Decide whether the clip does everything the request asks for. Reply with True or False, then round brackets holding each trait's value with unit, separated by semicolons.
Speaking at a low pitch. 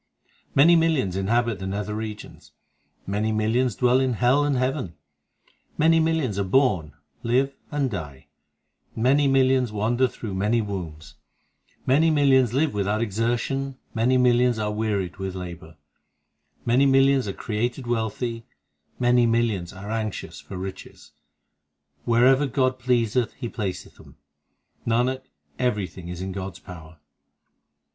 True (115 Hz)